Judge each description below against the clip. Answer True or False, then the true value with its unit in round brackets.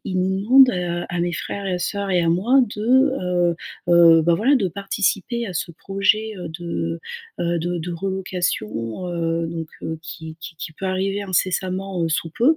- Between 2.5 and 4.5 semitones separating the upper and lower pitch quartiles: True (2.8 semitones)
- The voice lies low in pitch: False (180 Hz)